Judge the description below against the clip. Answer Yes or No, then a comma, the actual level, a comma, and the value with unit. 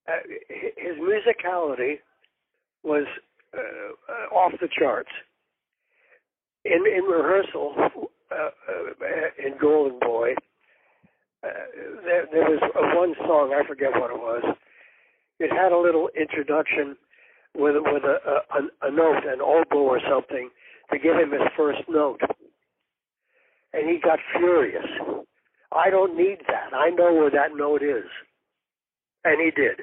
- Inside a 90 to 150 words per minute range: Yes, slow, 135 wpm